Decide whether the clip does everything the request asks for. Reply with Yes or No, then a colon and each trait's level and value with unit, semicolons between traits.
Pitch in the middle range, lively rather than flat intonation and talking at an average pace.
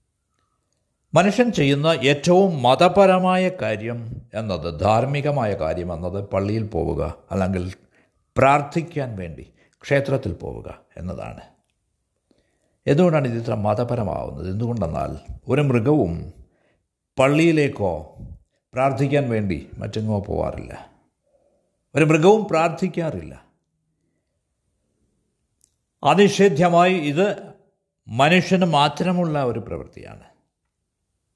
No: low, 130 Hz; wide, 8.7 semitones; average, 70 wpm